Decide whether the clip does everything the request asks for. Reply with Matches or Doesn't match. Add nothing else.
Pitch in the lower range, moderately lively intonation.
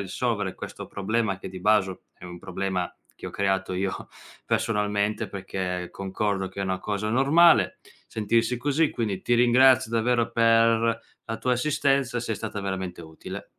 Matches